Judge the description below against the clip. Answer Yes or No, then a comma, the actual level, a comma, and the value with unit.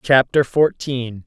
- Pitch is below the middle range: Yes, low, 130 Hz